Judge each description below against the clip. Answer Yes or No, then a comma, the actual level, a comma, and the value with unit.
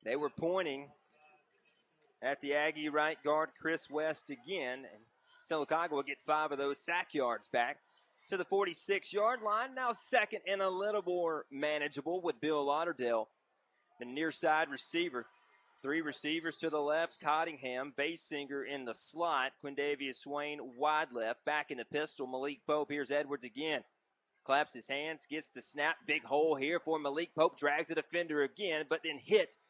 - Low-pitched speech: No, medium, 150 Hz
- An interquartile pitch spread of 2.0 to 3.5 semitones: Yes, narrow, 2.5 semitones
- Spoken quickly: No, average, 165 wpm